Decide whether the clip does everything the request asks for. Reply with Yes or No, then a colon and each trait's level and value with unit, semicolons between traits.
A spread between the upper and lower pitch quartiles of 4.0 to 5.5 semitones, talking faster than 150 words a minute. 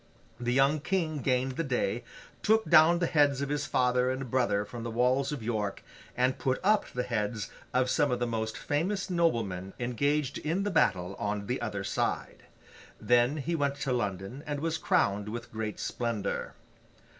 Yes: average, 4.7 semitones; average, 180 wpm